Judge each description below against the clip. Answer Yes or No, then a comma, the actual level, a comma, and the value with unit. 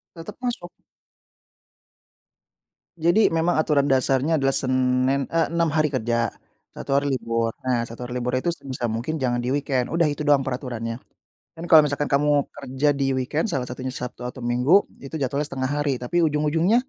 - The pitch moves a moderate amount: Yes, average, 3.3 semitones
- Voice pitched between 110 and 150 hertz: Yes, low, 135 Hz